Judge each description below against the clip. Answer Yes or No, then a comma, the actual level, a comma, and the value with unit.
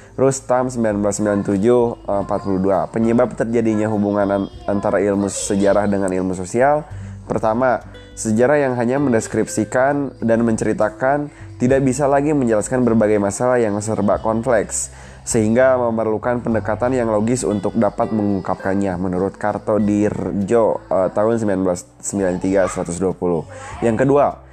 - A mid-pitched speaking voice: No, low, 105 Hz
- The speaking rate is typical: Yes, average, 105 wpm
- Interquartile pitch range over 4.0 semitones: No, average, 3.4 semitones